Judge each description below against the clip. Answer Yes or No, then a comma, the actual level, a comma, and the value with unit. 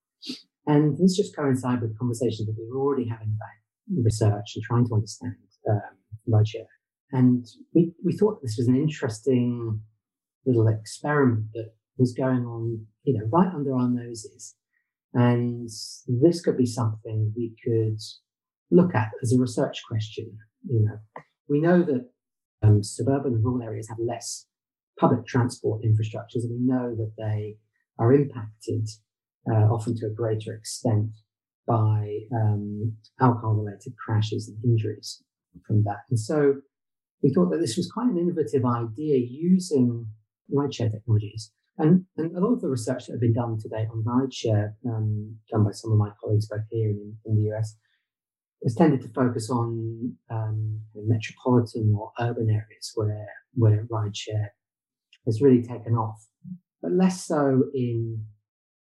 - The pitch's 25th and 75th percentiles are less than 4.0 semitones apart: Yes, average, 3.1 semitones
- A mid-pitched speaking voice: No, low, 115 Hz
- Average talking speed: Yes, average, 155 wpm